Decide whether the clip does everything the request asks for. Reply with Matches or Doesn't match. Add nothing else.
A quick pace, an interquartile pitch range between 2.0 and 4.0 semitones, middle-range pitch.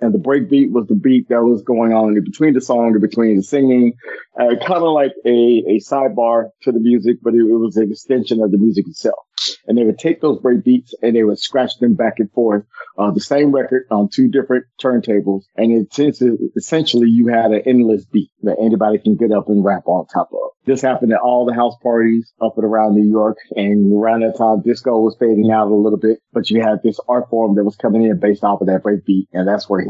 Doesn't match